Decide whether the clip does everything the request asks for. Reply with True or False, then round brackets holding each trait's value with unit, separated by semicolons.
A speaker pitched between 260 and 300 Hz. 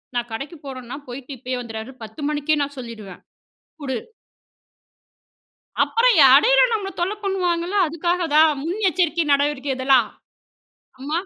True (290 Hz)